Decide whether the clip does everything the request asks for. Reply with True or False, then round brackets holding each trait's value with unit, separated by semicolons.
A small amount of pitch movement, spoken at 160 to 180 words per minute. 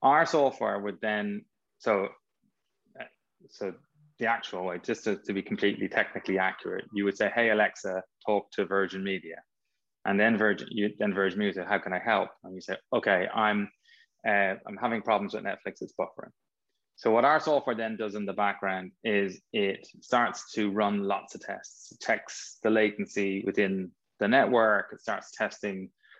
True (1.8 semitones; 175 wpm)